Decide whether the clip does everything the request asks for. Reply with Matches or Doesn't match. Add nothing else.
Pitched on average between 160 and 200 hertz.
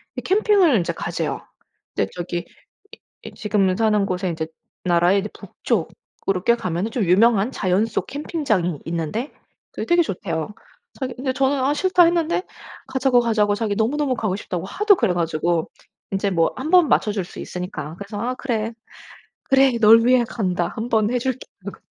Doesn't match